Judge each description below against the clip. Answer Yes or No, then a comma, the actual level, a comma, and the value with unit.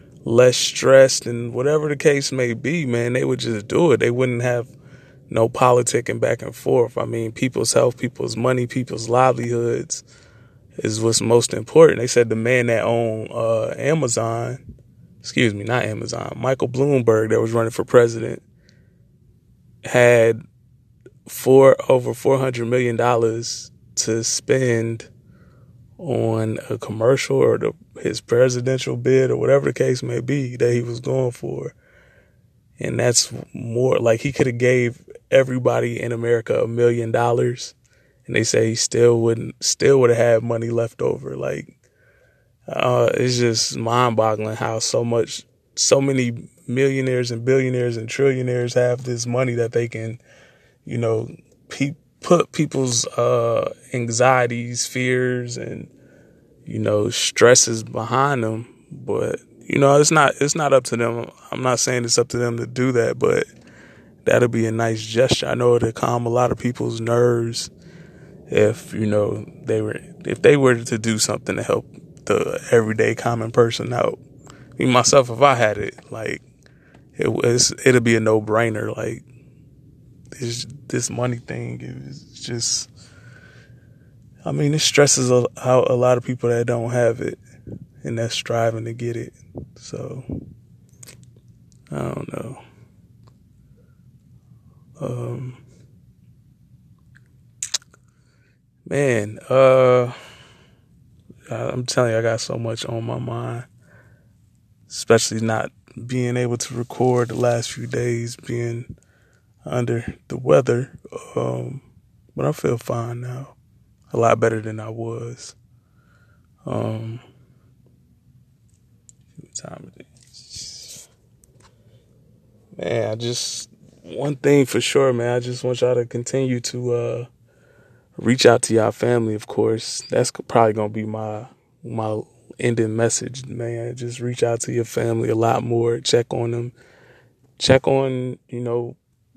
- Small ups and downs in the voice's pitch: Yes, narrow, 1.7 semitones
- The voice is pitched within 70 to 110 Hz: No, low, 120 Hz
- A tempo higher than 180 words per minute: No, average, 140 wpm